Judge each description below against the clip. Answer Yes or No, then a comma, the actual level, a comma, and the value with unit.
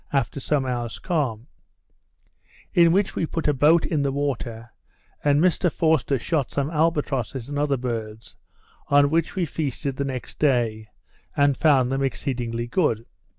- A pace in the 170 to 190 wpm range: No, average, 150 wpm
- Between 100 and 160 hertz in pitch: Yes, medium, 140 Hz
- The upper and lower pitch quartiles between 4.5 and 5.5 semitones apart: No, average, 3.8 semitones